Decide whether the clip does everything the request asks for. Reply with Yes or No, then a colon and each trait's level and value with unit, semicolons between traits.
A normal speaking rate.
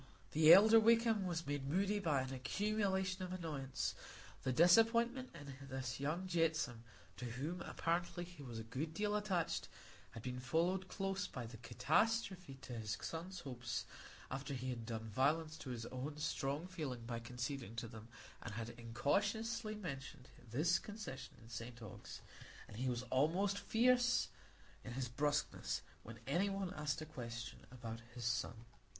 Yes: average, 160 wpm